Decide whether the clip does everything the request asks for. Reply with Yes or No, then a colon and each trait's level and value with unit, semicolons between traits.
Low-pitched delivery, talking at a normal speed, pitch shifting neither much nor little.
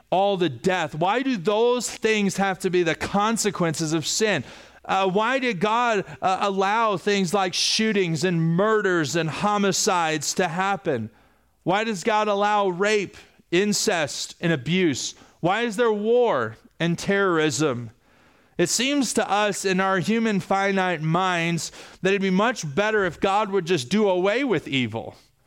No: high, 195 Hz; average, 155 wpm; average, 3.8 semitones